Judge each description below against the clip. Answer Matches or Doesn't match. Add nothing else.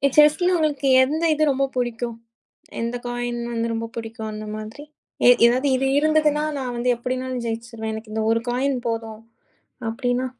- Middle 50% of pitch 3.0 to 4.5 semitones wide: Matches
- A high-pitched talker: Matches